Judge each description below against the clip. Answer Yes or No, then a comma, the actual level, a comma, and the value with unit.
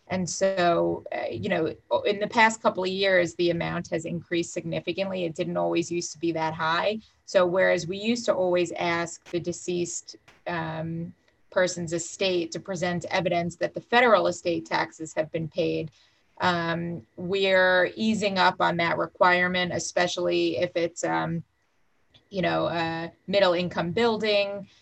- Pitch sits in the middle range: Yes, medium, 175 Hz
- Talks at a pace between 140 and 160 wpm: Yes, average, 155 wpm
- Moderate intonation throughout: No, narrow, 1.9 semitones